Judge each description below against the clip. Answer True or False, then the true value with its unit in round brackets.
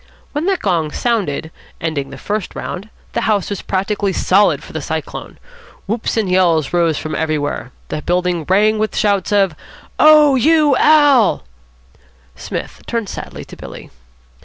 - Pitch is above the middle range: True (200 Hz)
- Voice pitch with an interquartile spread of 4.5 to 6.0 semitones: True (5.3 semitones)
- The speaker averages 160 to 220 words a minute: False (150 wpm)